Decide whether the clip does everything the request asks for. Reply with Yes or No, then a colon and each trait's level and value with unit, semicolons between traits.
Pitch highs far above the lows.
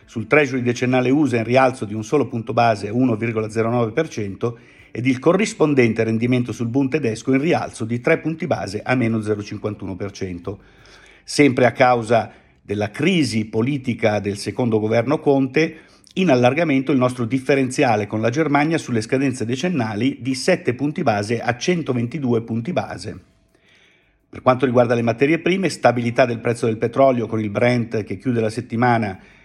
No: average, 3.4 semitones